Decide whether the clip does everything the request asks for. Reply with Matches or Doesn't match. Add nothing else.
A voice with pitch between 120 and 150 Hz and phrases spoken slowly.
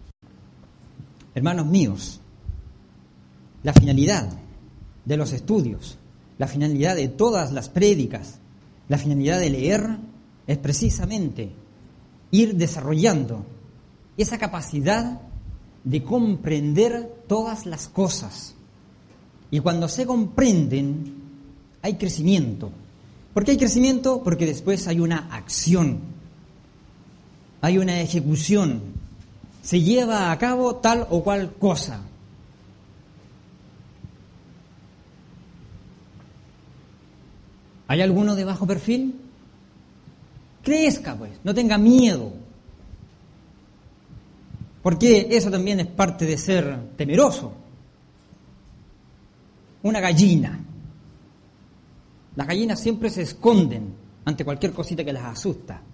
Doesn't match